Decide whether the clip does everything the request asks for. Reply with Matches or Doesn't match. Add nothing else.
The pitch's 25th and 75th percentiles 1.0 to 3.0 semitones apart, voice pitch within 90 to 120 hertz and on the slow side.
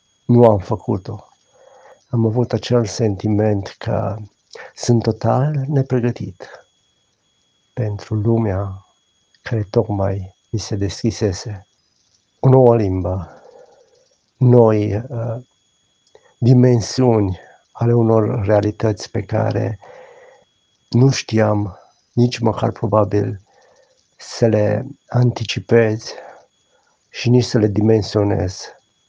Matches